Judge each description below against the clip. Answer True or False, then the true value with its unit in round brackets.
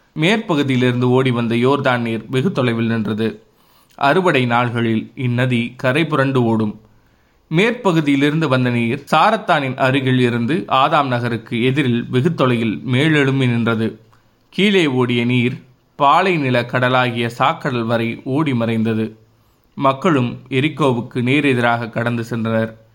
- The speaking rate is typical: True (105 wpm)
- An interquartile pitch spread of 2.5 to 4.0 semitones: True (2.8 semitones)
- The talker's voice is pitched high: False (125 Hz)